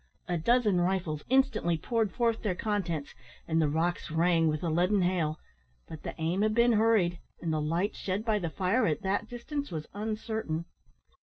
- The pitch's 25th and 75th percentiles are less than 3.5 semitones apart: No, average, 5.0 semitones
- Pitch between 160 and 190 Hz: Yes, medium, 185 Hz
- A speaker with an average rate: Yes, average, 180 wpm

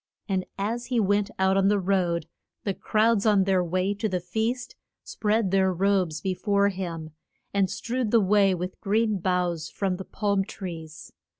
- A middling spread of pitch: No, narrow, 2.3 semitones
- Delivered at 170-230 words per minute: Yes, average, 175 wpm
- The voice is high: Yes, high, 195 Hz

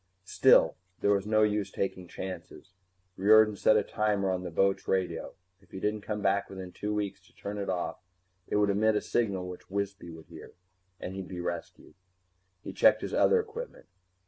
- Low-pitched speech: Yes, low, 100 Hz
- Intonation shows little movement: Yes, narrow, 2.0 semitones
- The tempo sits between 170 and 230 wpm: Yes, average, 190 wpm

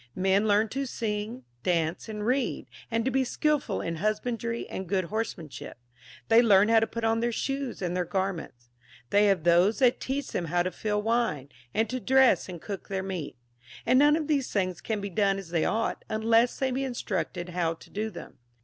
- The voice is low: No, high, 210 Hz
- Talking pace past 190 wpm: Yes, fast, 205 wpm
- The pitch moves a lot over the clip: No, average, 4.5 semitones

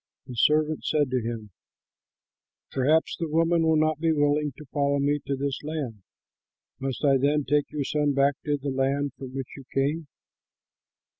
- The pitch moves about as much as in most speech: No, narrow, 2.1 semitones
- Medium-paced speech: Yes, average, 170 wpm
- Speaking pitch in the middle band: Yes, medium, 145 Hz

